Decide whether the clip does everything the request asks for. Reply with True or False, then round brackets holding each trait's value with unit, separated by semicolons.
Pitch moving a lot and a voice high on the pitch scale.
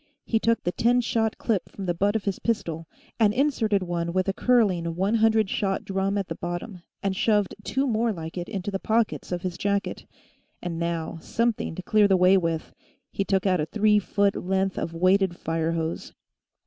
False (3.7 semitones; 195 Hz)